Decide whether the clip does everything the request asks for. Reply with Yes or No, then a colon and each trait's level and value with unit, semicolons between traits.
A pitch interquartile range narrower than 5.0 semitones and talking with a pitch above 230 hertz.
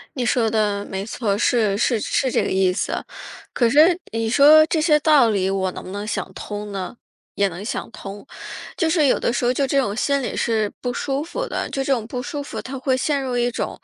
No: average, 5.3 semitones; high, 240 Hz